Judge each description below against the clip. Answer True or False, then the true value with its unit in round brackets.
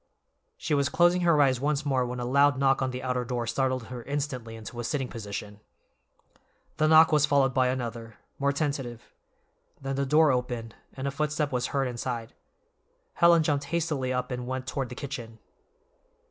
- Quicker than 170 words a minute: True (180 wpm)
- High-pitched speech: False (130 Hz)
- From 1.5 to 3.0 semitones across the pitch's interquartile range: True (2.6 semitones)